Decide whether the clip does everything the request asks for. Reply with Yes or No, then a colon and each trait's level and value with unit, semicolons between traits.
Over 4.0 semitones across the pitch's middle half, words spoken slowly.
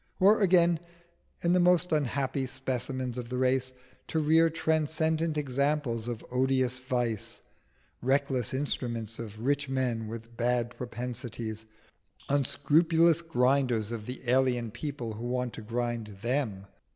No: average, 3.6 semitones; slow, 125 wpm